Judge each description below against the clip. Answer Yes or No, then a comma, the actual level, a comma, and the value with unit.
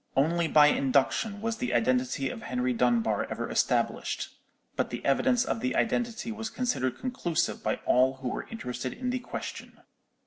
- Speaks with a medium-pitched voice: Yes, medium, 150 Hz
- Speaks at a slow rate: No, average, 165 wpm